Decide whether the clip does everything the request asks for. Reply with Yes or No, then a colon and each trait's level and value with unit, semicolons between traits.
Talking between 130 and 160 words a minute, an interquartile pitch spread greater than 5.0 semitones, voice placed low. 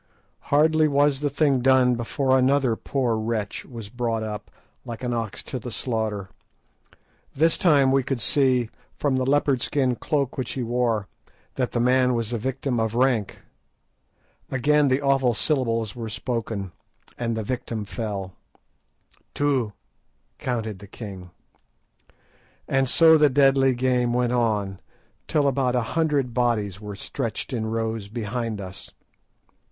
No: average, 145 wpm; average, 3.2 semitones; low, 125 Hz